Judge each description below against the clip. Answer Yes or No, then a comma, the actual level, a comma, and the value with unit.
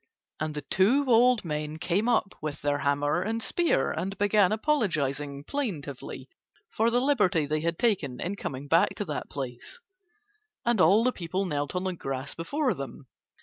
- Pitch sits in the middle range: Yes, medium, 180 Hz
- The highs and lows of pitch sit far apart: Yes, wide, 7.4 semitones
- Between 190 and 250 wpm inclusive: No, average, 170 wpm